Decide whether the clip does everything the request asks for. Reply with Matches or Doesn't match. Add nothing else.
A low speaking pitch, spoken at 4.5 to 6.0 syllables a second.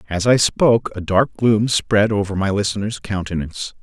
Matches